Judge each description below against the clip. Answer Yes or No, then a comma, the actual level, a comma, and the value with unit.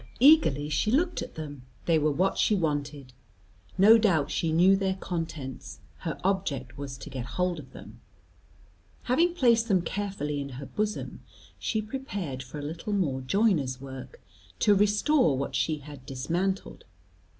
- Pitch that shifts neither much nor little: No, wide, 6.6 semitones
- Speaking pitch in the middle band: Yes, medium, 170 Hz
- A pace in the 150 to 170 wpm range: Yes, average, 155 wpm